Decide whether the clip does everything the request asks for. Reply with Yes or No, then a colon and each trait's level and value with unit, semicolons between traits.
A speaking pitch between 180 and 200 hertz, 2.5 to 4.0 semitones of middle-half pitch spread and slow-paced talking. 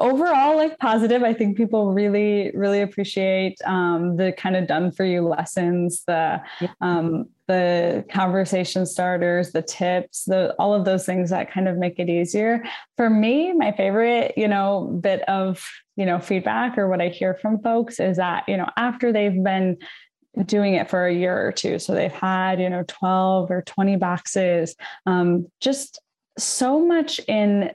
No: high, 190 Hz; average, 2.8 semitones; average, 170 wpm